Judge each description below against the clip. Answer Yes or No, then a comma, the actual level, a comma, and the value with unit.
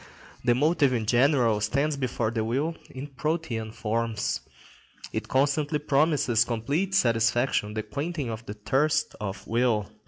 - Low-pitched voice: Yes, low, 125 Hz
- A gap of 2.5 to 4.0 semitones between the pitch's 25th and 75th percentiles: No, average, 4.7 semitones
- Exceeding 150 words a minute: No, slow, 135 wpm